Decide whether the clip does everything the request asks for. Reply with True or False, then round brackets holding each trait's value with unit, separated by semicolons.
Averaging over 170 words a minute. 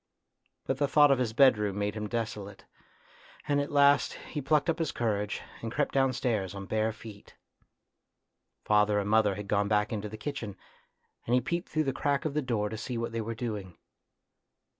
True (190 wpm)